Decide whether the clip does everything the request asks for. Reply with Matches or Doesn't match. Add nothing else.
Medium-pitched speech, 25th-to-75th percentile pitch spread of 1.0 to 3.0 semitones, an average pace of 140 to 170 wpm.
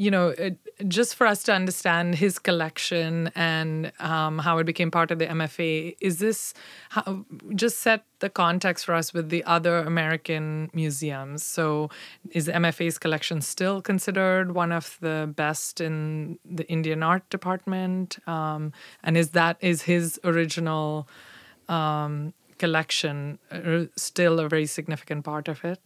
Matches